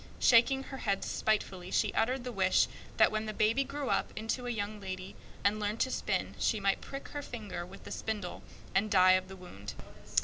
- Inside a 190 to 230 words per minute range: Yes, fast, 205 wpm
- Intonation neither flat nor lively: Yes, average, 4.1 semitones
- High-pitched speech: Yes, high, 215 Hz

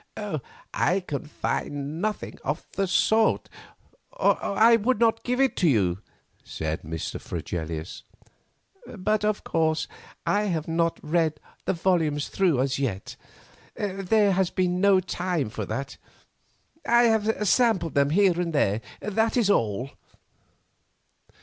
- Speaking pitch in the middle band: Yes, medium, 180 Hz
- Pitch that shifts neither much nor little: No, wide, 6.7 semitones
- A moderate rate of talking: No, slow, 130 wpm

